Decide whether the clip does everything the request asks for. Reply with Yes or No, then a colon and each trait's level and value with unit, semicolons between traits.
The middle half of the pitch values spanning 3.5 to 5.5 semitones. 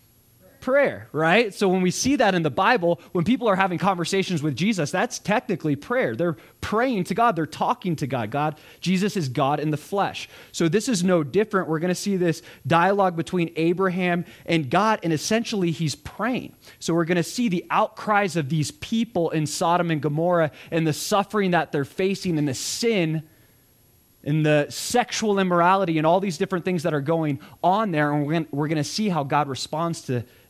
Yes: average, 4.2 semitones